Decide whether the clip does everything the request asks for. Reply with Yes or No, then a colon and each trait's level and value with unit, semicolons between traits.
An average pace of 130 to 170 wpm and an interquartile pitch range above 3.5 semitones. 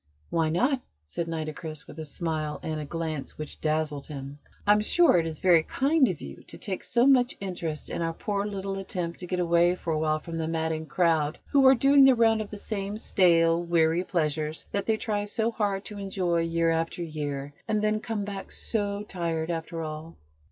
No: fast, 205 wpm; average, 4.4 semitones